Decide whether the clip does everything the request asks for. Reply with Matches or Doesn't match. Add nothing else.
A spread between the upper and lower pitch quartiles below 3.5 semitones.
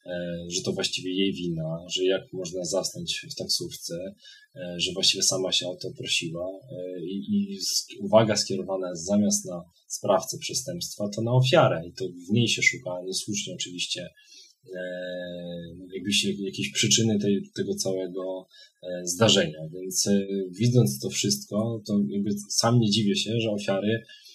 Doesn't match